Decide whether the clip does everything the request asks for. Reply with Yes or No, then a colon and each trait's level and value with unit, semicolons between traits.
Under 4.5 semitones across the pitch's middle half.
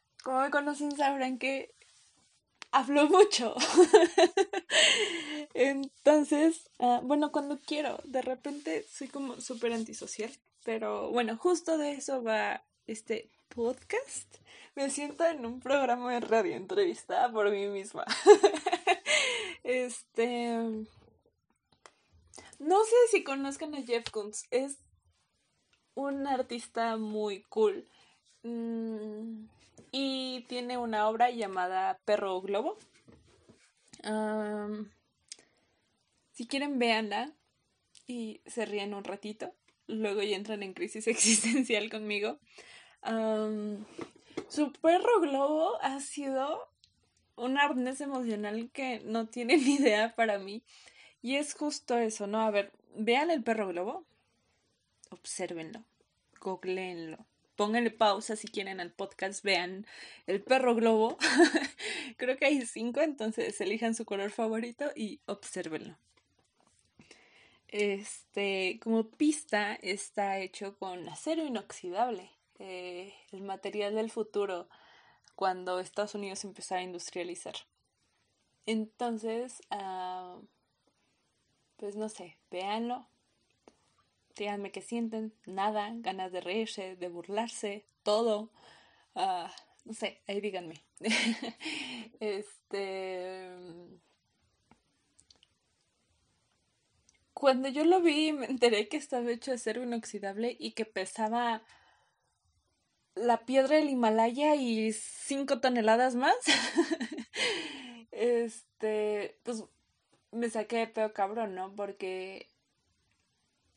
No: average, 5.1 semitones